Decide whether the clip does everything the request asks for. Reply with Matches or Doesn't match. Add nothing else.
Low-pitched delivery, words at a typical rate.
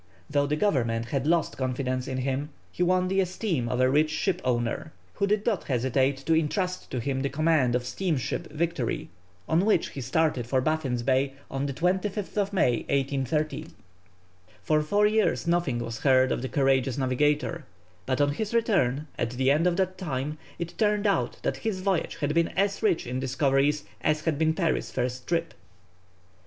Doesn't match